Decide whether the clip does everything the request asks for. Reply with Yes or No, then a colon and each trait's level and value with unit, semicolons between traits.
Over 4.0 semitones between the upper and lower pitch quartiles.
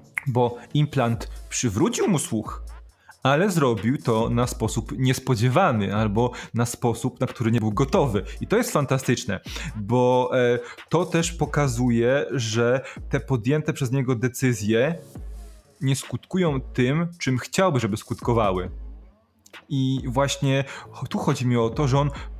No: average, 3.2 semitones